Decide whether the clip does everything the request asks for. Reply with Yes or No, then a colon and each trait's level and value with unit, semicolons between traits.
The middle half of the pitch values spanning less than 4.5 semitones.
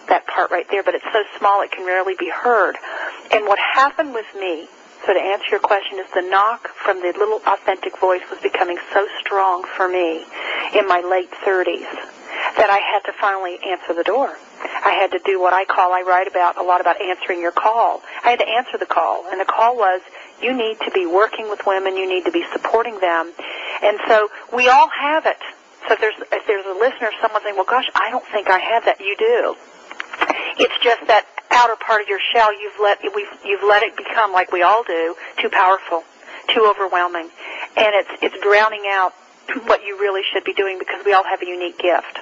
Yes: average, 3.4 semitones